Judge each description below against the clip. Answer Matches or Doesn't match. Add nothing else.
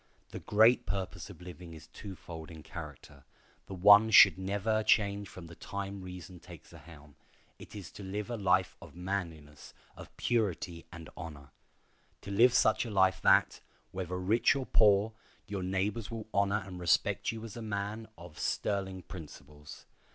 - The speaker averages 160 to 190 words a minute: Matches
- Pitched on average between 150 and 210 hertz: Doesn't match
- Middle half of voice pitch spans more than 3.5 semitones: Doesn't match